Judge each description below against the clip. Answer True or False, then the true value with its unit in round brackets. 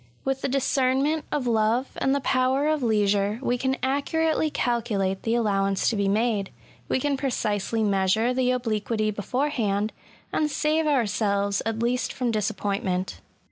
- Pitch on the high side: True (235 Hz)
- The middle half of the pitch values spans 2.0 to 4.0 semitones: False (4.6 semitones)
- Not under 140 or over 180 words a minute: True (160 wpm)